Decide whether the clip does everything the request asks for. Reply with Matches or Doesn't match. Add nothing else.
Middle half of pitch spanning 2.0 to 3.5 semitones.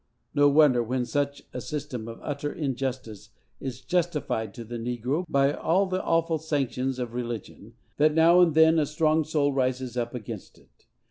Doesn't match